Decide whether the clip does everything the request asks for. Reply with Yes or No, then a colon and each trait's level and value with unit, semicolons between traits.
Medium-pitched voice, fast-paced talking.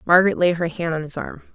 Yes: medium, 170 Hz; fast, 270 wpm